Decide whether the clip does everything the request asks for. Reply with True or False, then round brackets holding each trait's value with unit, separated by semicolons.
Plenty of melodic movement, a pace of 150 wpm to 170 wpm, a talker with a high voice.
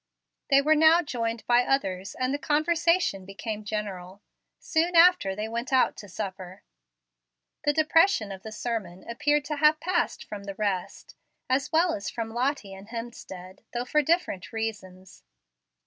True (7.1 semitones; 155 wpm; 230 Hz)